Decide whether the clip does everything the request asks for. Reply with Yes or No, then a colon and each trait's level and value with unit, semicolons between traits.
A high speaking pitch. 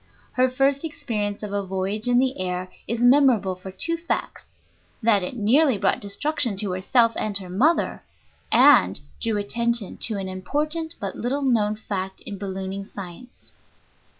Yes: high, 210 Hz